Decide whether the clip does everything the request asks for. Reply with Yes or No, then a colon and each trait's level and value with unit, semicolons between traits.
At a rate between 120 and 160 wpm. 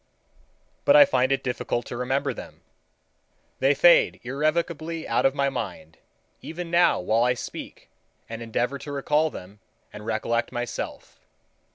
Yes: average, 145 wpm